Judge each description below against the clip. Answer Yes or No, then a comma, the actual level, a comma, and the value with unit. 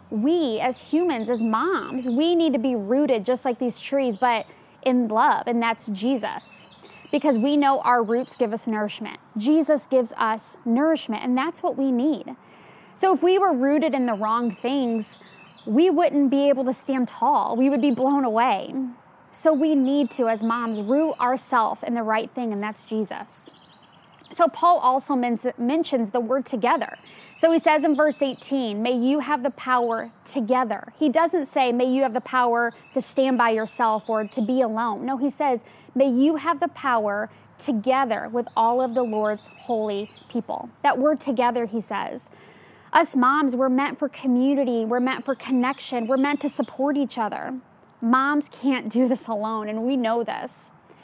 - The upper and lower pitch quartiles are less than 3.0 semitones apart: No, average, 3.3 semitones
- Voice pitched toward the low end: No, very high, 255 Hz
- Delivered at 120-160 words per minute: No, average, 180 wpm